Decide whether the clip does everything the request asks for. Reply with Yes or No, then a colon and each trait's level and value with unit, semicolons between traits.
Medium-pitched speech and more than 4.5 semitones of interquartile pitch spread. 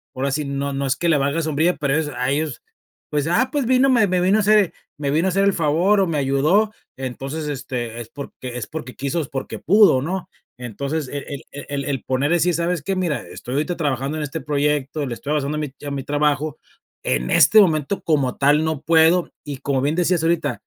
No: medium, 150 Hz; average, 3.7 semitones